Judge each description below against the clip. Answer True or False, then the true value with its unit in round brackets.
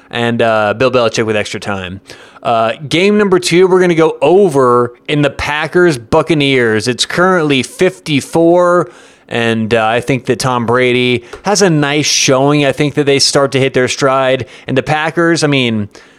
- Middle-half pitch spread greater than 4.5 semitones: True (5.0 semitones)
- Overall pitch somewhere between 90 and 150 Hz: True (135 Hz)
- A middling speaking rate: True (180 wpm)